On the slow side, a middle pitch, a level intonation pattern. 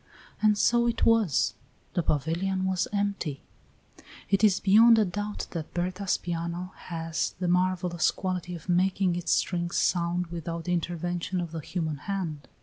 No: average, 150 wpm; medium, 180 Hz; narrow, 2.2 semitones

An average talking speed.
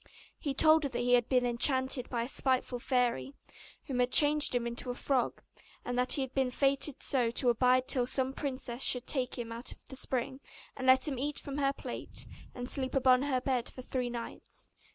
No: fast, 215 wpm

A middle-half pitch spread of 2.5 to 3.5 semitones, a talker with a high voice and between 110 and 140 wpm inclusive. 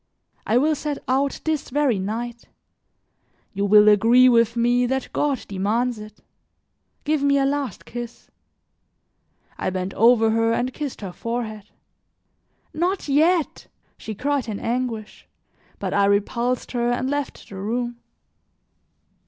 No: average, 4.0 semitones; high, 240 Hz; slow, 135 wpm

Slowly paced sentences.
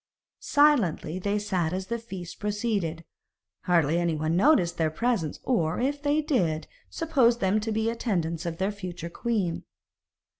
No: average, 145 wpm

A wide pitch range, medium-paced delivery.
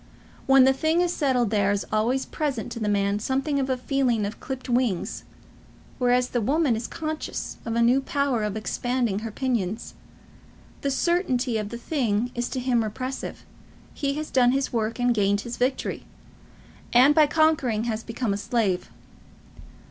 No: average, 3.5 semitones; average, 170 wpm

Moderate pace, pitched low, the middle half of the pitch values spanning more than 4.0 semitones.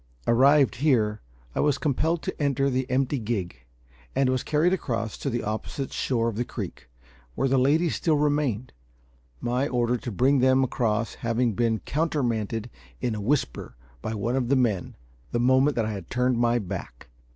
No: average, 175 wpm; low, 125 Hz; average, 3.4 semitones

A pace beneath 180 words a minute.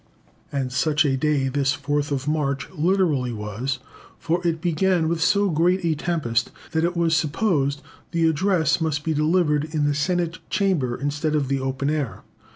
Yes: average, 170 wpm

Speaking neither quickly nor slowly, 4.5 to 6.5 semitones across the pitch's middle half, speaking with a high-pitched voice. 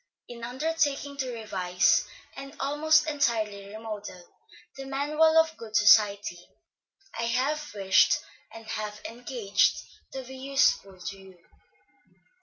No: slow, 115 wpm; average, 5.2 semitones; high, 235 Hz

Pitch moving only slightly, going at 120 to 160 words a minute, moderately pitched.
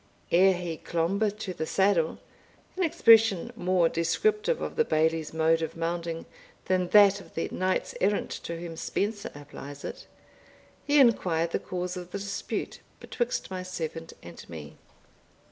No: average, 3.7 semitones; average, 150 wpm; medium, 180 Hz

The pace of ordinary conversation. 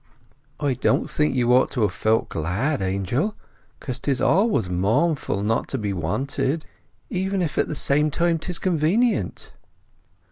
Yes: average, 150 wpm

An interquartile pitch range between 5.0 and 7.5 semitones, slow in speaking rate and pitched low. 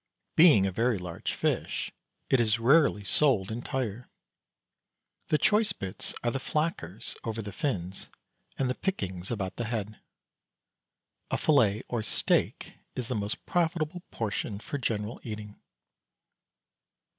Yes: average, 5.3 semitones; slow, 130 wpm; low, 115 Hz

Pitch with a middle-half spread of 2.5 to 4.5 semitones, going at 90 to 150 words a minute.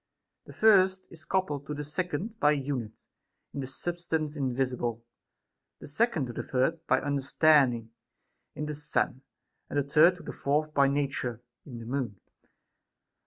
No: average, 3.3 semitones; average, 160 wpm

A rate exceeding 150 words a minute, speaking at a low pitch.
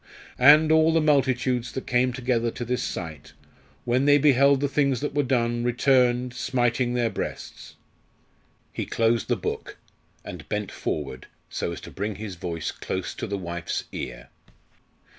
Yes: average, 160 wpm; low, 125 Hz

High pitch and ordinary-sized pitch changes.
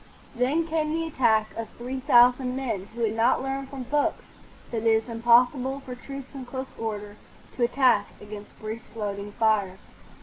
Yes: high, 245 Hz; average, 3.4 semitones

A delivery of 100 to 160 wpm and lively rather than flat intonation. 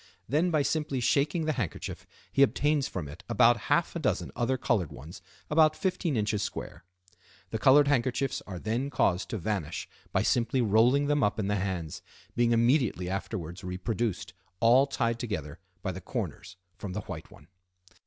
No: average, 170 wpm; wide, 6.2 semitones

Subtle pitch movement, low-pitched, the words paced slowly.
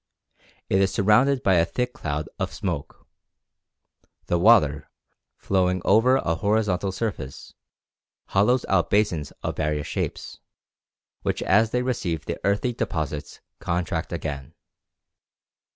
No: average, 5.3 semitones; very low, 95 Hz; slow, 120 wpm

